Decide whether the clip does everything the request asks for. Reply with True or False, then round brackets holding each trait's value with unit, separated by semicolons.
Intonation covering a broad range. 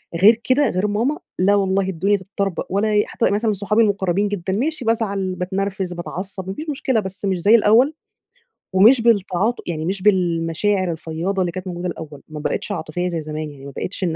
False (3.0 semitones)